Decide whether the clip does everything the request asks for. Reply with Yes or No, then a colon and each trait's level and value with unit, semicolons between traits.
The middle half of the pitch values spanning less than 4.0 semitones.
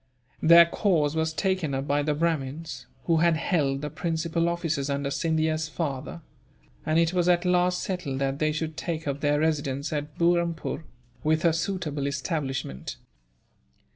Yes: average, 2.8 semitones